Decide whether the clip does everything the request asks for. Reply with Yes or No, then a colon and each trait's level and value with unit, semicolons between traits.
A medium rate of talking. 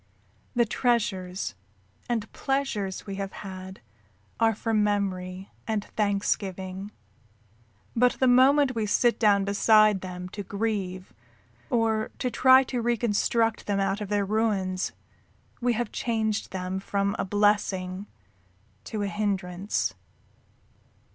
No: slow, 120 wpm